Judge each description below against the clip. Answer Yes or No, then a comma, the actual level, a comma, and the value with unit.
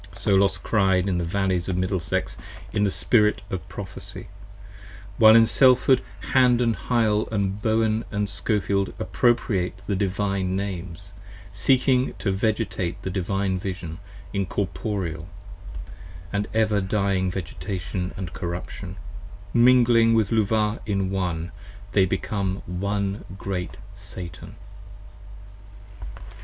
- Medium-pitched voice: No, low, 100 Hz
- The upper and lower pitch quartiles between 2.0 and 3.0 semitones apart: Yes, narrow, 2.6 semitones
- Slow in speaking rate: Yes, slow, 120 wpm